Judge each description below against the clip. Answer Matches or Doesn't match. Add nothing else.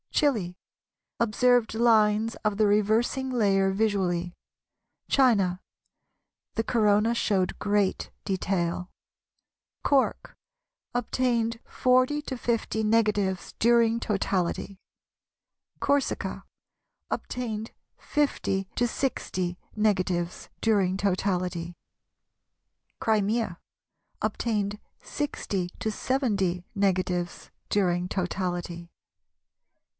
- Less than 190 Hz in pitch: Doesn't match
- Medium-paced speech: Doesn't match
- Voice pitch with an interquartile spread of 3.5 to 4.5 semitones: Matches